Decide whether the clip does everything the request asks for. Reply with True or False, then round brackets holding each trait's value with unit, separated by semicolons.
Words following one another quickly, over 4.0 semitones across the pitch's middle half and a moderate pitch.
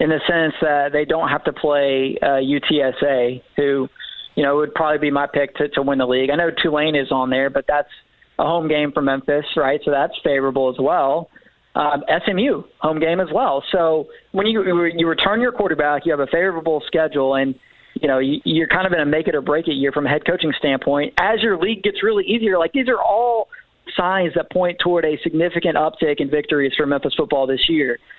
False (220 wpm; 3.2 semitones; 150 Hz)